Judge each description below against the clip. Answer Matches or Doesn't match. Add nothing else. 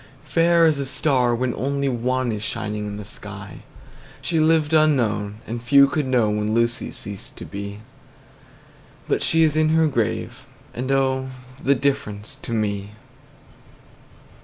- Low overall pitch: Matches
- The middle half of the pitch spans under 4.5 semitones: Doesn't match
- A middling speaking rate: Matches